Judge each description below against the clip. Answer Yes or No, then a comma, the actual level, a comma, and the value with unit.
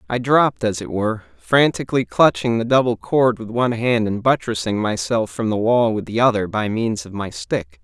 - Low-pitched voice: Yes, low, 115 Hz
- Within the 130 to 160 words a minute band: No, fast, 205 wpm